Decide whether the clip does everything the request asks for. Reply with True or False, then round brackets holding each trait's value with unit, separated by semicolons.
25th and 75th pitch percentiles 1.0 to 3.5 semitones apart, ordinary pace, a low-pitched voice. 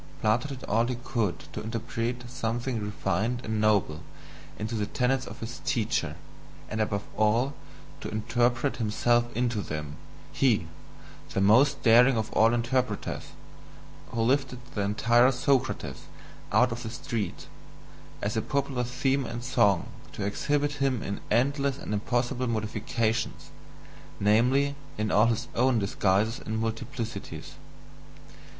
False (2.8 semitones; 130 wpm; 115 Hz)